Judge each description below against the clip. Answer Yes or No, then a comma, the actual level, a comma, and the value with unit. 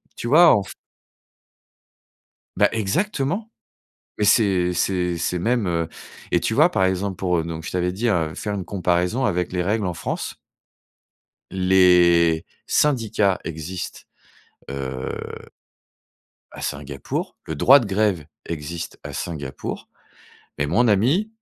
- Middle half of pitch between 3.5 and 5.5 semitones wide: Yes, average, 4.2 semitones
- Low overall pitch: Yes, very low, 90 Hz